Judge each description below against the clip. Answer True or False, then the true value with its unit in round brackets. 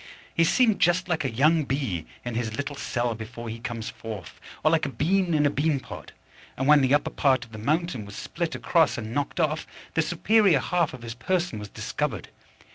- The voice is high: False (140 Hz)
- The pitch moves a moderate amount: False (5.9 semitones)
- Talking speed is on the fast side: True (210 wpm)